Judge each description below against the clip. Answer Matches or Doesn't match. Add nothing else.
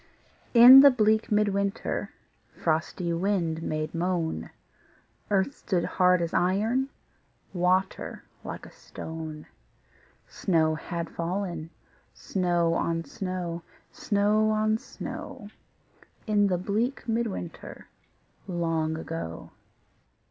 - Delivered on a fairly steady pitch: Doesn't match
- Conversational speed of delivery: Doesn't match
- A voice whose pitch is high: Doesn't match